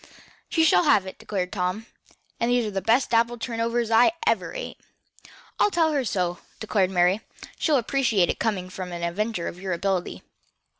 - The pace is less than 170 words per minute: No, average, 180 wpm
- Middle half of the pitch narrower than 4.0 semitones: No, average, 4.7 semitones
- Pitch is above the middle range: Yes, high, 215 Hz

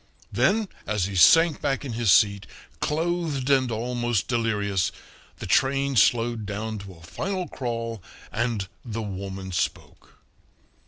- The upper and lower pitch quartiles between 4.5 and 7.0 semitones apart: Yes, average, 5.1 semitones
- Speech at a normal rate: No, slow, 130 wpm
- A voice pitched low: Yes, low, 115 Hz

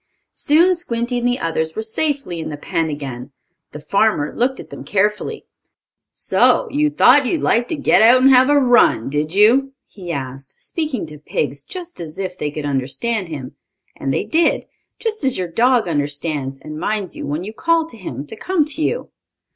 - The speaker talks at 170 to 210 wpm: Yes, average, 195 wpm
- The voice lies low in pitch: No, high, 210 Hz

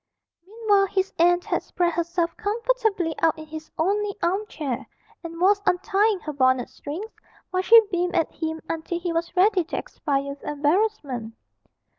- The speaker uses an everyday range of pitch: Yes, average, 4.2 semitones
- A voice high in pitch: Yes, very high, 350 Hz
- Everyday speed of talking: Yes, average, 160 wpm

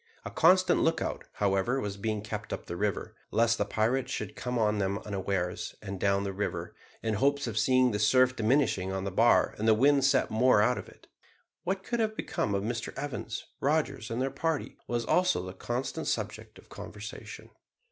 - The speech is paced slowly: No, average, 195 wpm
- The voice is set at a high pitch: No, low, 115 Hz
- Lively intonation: No, average, 5.0 semitones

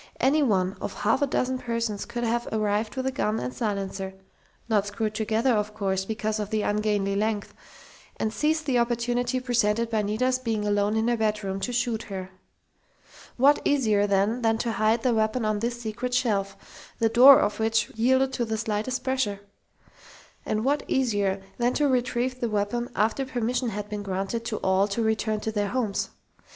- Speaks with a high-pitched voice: Yes, high, 220 Hz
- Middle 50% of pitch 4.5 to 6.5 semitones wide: No, average, 2.8 semitones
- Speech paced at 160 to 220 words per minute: Yes, average, 185 wpm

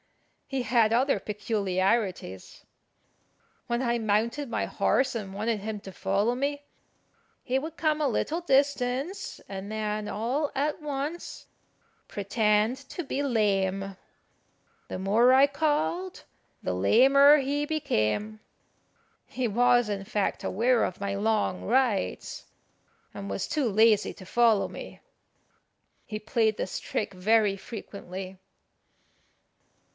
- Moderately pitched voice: No, high, 225 Hz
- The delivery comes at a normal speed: No, slow, 120 wpm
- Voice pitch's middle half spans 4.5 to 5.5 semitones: Yes, average, 5.2 semitones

